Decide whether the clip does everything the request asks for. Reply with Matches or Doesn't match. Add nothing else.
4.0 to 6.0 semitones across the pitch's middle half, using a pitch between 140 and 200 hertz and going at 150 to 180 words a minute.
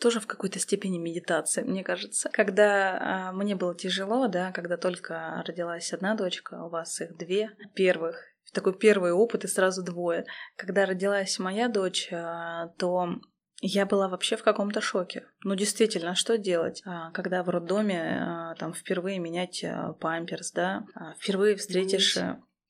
Doesn't match